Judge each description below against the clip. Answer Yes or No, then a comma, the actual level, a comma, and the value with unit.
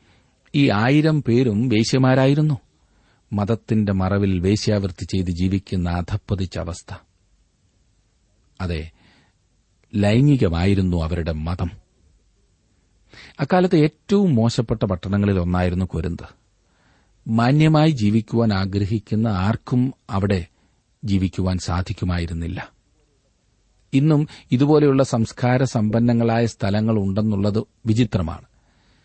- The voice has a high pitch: No, low, 105 Hz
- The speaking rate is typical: Yes, average, 70 wpm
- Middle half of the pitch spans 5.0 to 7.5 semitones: No, average, 4.5 semitones